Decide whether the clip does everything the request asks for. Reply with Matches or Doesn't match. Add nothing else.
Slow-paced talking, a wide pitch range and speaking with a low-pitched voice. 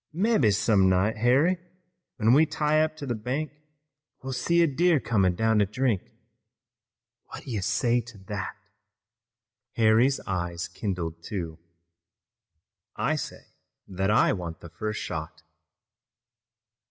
Matches